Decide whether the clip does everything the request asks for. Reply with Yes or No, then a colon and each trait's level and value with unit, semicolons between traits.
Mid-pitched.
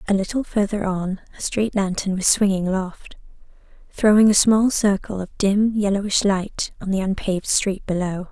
No: high, 200 Hz